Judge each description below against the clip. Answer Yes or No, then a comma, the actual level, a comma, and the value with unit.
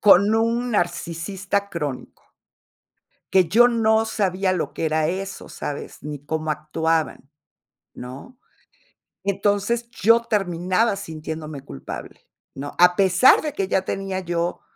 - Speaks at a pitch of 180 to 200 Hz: Yes, medium, 185 Hz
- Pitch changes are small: No, average, 4.5 semitones